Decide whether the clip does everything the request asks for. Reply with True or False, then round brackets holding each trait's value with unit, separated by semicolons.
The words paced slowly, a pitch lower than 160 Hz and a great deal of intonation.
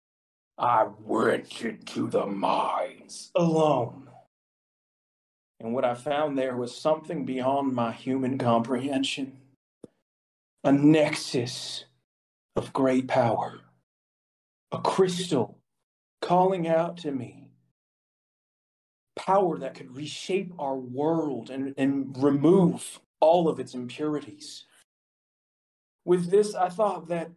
False (100 wpm; 140 Hz; 4.2 semitones)